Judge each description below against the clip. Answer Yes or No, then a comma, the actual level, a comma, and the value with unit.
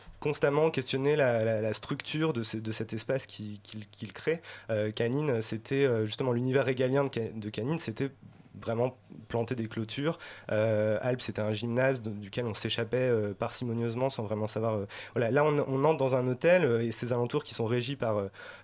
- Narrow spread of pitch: No, average, 3.4 semitones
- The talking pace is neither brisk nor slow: Yes, average, 180 wpm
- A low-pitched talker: Yes, low, 115 Hz